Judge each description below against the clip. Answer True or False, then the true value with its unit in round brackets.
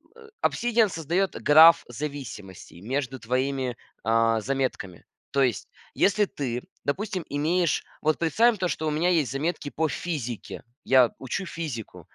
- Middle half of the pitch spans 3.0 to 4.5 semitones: False (5.3 semitones)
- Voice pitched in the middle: True (145 Hz)